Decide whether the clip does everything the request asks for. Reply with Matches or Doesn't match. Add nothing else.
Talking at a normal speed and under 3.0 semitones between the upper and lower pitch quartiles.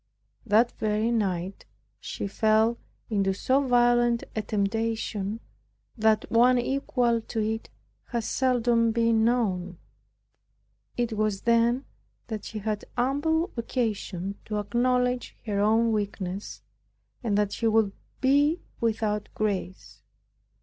Doesn't match